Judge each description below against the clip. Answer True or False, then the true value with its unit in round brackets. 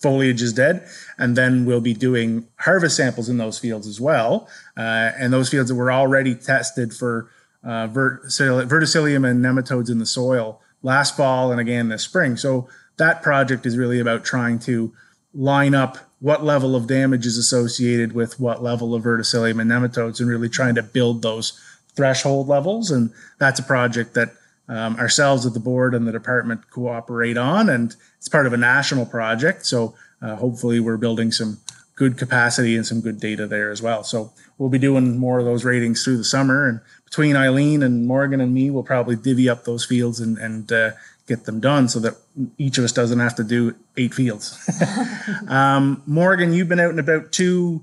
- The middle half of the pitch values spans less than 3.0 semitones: True (2.5 semitones)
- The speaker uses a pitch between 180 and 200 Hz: False (125 Hz)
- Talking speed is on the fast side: False (195 wpm)